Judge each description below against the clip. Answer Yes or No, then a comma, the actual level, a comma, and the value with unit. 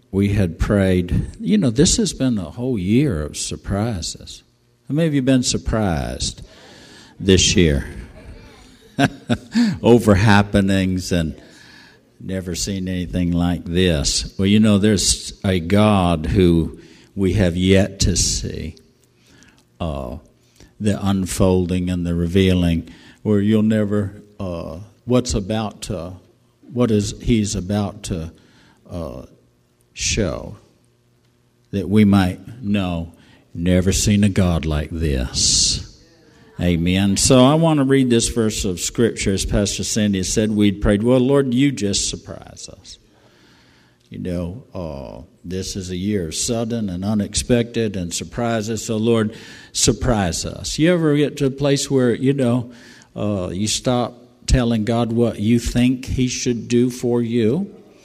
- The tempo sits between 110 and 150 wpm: Yes, slow, 135 wpm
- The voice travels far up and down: No, average, 4.8 semitones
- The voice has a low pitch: Yes, low, 100 Hz